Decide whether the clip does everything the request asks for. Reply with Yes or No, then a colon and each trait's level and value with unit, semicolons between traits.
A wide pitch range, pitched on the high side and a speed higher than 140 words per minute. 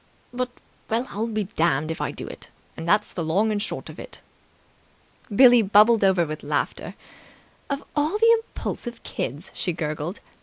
Yes: wide, 6.1 semitones; high, 210 Hz; average, 165 wpm